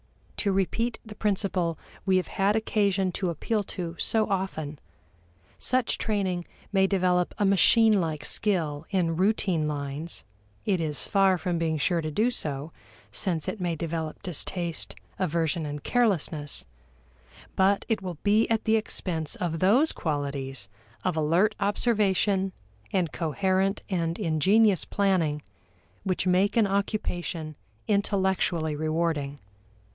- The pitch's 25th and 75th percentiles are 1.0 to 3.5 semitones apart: No, average, 3.9 semitones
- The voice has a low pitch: No, medium, 185 Hz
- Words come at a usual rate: No, slow, 130 wpm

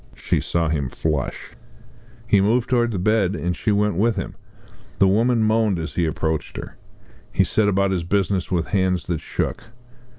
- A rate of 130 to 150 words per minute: No, average, 175 wpm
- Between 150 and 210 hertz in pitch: No, very low, 95 Hz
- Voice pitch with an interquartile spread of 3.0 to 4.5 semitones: Yes, average, 3.9 semitones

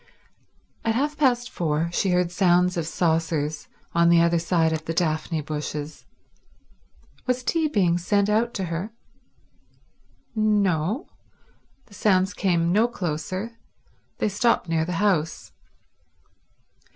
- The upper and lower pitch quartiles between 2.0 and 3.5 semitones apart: No, average, 4.3 semitones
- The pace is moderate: No, slow, 125 wpm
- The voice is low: No, medium, 180 Hz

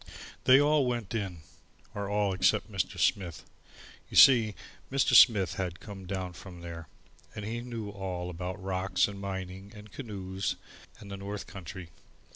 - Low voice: Yes, low, 100 Hz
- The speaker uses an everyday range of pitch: No, narrow, 2.3 semitones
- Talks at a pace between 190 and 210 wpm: No, average, 155 wpm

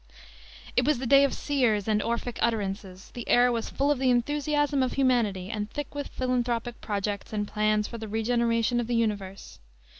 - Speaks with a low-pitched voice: No, high, 235 Hz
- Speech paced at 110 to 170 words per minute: No, average, 185 wpm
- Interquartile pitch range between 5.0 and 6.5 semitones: No, average, 3.3 semitones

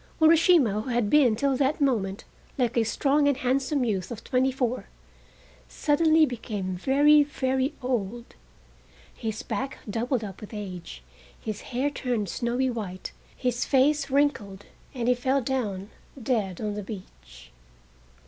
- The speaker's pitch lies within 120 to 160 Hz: No, high, 245 Hz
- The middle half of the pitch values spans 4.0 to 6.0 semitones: Yes, average, 4.6 semitones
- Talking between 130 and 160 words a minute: Yes, average, 140 wpm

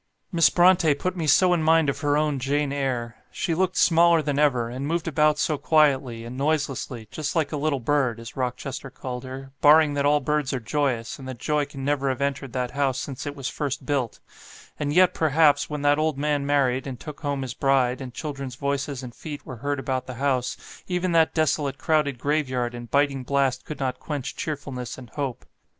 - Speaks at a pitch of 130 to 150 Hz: Yes, medium, 140 Hz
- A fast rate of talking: Yes, fast, 210 wpm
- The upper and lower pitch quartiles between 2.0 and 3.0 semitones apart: Yes, narrow, 2.6 semitones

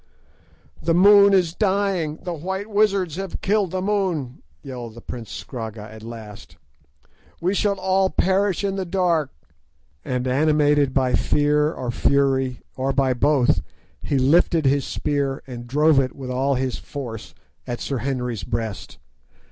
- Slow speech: No, average, 145 wpm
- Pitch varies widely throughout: Yes, wide, 6.5 semitones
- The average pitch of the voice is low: No, medium, 145 Hz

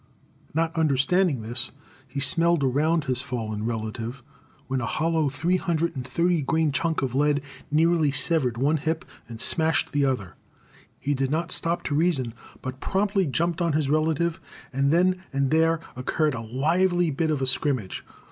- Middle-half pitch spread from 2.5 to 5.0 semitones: Yes, average, 4.1 semitones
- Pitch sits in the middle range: Yes, medium, 150 Hz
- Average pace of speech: Yes, average, 165 wpm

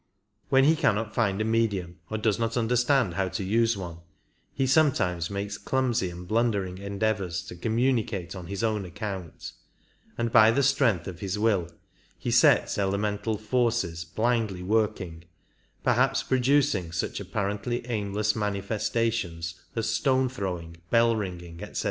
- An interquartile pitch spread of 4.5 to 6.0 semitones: No, average, 3.9 semitones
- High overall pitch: No, low, 105 Hz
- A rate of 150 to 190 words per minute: No, average, 140 wpm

